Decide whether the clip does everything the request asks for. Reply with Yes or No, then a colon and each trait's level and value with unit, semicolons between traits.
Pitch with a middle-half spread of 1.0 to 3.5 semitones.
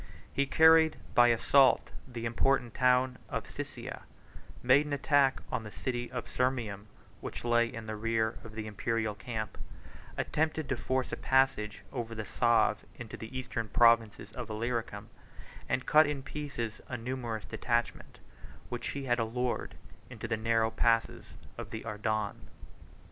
Yes: average, 2.7 semitones